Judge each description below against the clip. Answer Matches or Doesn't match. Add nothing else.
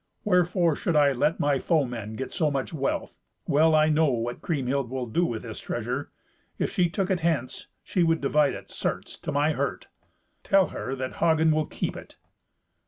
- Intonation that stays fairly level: Doesn't match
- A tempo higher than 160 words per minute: Matches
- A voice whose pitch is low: Doesn't match